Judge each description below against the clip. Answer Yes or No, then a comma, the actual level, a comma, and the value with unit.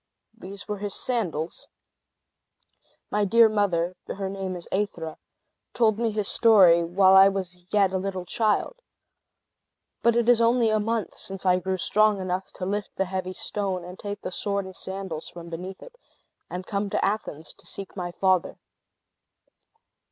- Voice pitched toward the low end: No, high, 195 Hz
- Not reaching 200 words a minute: Yes, average, 165 wpm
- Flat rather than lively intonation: Yes, narrow, 2.3 semitones